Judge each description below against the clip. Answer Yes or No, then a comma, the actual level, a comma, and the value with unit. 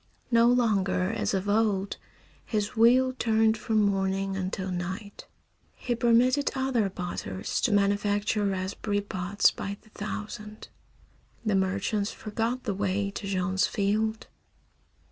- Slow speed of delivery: Yes, slow, 125 wpm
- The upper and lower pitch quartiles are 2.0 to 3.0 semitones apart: Yes, narrow, 2.5 semitones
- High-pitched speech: Yes, high, 205 Hz